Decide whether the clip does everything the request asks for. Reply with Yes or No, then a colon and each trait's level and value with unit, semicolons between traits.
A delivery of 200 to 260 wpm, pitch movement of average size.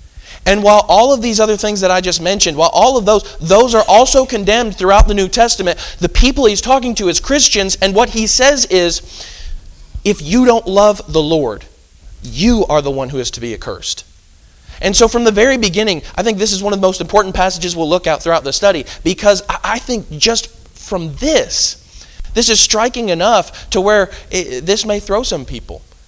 No: fast, 205 wpm; wide, 6.1 semitones